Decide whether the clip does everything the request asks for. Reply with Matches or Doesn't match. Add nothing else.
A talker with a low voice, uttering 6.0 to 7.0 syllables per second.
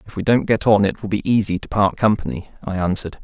Matches